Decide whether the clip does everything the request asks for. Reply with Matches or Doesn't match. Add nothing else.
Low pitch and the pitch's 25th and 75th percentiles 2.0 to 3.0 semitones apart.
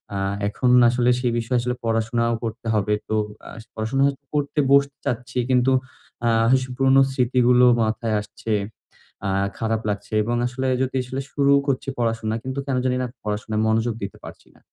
Matches